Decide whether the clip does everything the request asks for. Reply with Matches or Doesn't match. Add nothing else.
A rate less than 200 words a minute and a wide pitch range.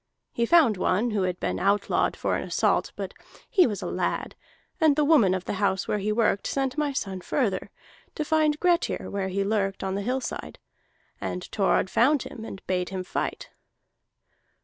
Matches